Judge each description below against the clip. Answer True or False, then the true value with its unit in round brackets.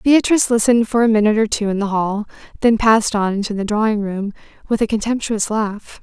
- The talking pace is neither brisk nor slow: False (210 wpm)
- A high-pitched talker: True (215 Hz)